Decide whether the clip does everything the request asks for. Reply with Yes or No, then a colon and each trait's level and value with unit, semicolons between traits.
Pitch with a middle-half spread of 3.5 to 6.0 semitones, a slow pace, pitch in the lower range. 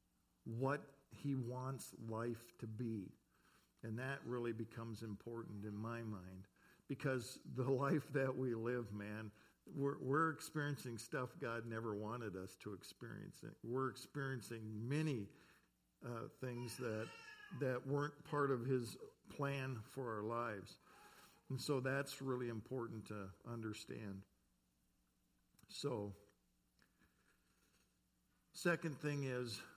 Yes: average, 4.0 semitones; slow, 115 wpm; low, 120 Hz